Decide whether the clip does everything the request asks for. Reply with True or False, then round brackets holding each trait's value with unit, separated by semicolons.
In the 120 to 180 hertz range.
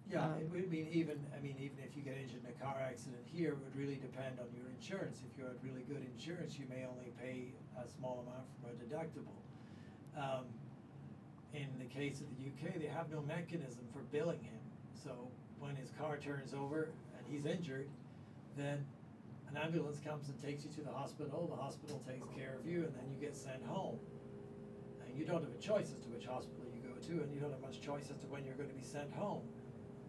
True (140 Hz)